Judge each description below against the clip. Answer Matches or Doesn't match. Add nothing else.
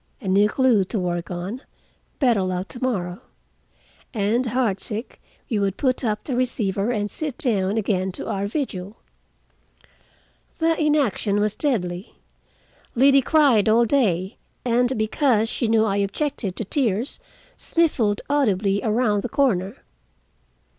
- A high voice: Matches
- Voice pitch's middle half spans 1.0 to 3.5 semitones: Doesn't match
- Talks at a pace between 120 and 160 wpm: Matches